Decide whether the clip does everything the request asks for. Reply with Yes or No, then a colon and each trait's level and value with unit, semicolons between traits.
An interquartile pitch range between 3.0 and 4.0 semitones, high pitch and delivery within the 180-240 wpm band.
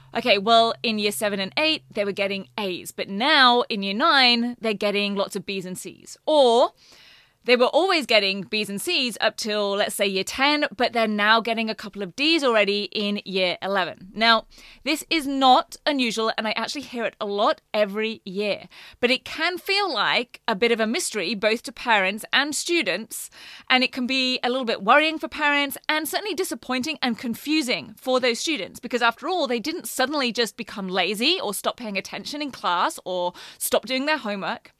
No: average, 5.2 semitones; high, 235 Hz; average, 200 wpm